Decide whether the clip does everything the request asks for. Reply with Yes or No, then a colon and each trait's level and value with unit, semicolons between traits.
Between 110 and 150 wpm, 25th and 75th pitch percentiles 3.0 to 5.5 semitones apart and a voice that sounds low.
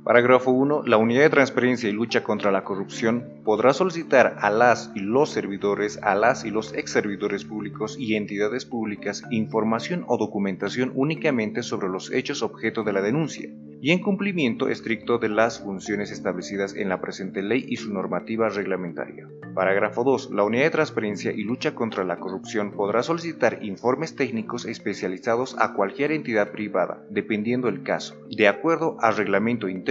No: average, 165 wpm; average, 3.7 semitones; low, 110 Hz